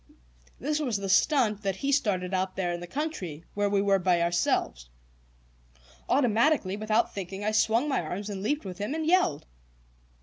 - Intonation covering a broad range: Yes, wide, 5.7 semitones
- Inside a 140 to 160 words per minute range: No, average, 175 wpm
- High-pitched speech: Yes, high, 205 Hz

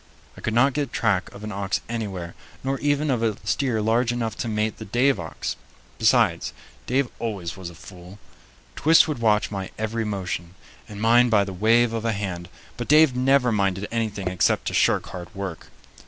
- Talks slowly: No, average, 190 wpm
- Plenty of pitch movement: No, average, 3.8 semitones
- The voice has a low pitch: Yes, low, 110 Hz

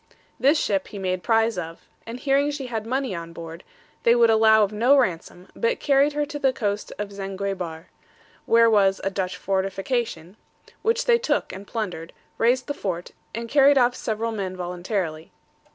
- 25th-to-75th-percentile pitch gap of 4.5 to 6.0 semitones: Yes, average, 5.3 semitones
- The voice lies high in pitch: Yes, high, 215 Hz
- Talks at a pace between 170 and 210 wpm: Yes, average, 175 wpm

